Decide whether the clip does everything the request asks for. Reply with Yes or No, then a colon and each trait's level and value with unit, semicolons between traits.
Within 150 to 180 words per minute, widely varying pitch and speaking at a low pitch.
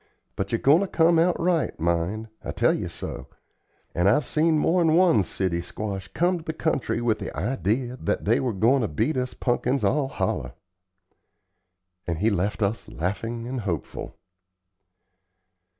Yes: average, 165 wpm; wide, 7.5 semitones; low, 115 Hz